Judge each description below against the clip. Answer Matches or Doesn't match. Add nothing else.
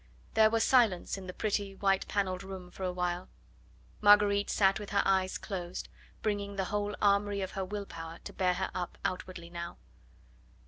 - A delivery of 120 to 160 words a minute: Doesn't match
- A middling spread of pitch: Doesn't match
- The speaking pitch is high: Matches